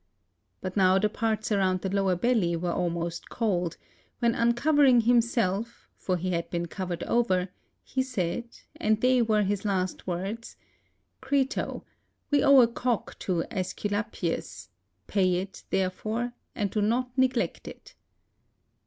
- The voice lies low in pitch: No, high, 205 Hz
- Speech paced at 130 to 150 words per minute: Yes, average, 140 wpm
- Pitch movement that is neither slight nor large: Yes, average, 4.5 semitones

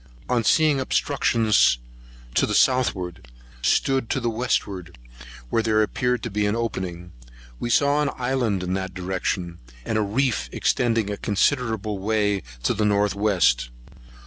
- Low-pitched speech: Yes, low, 105 Hz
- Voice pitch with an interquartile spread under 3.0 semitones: No, average, 4.4 semitones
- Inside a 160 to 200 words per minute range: No, average, 145 wpm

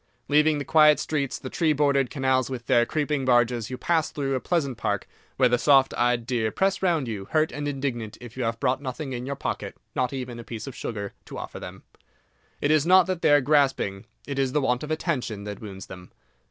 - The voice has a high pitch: No, low, 135 Hz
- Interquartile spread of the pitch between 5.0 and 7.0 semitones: No, average, 3.6 semitones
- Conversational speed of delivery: No, fast, 215 wpm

